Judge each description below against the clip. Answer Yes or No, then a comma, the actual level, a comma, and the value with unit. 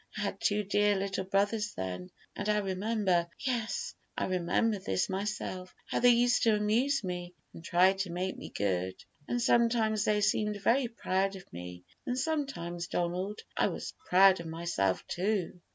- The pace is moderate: Yes, average, 170 wpm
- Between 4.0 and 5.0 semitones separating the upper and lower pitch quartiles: No, average, 3.6 semitones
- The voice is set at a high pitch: Yes, high, 195 Hz